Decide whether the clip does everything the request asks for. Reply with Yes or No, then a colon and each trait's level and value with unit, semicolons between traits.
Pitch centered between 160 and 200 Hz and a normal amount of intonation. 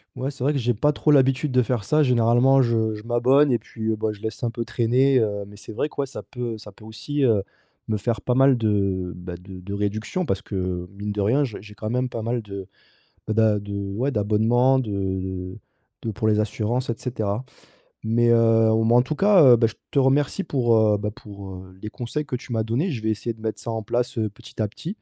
No: low, 115 Hz; average, 3.3 semitones